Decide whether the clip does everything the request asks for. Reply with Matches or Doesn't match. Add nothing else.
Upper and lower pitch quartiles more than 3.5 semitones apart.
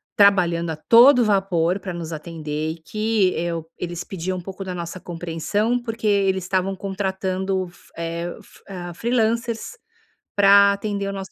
Doesn't match